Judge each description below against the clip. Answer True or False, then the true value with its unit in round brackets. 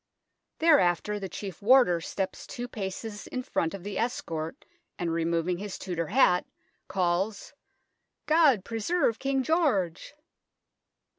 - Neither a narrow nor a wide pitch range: False (6.1 semitones)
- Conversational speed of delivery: False (125 wpm)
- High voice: True (200 Hz)